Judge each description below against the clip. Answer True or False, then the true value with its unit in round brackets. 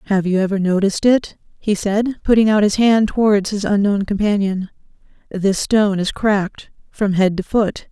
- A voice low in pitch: False (205 Hz)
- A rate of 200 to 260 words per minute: False (175 wpm)